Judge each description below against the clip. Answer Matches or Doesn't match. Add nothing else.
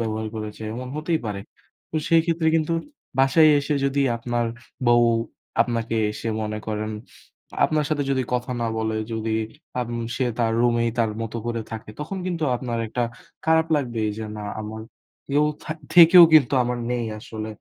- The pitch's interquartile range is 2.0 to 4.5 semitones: Doesn't match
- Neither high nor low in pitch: Doesn't match